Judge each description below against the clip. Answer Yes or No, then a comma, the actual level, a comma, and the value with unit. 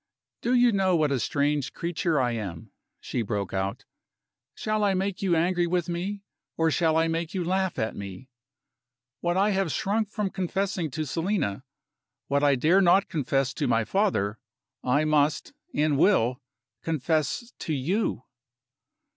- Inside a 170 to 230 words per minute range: No, average, 155 wpm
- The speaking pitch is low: No, medium, 165 Hz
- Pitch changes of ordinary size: No, wide, 5.9 semitones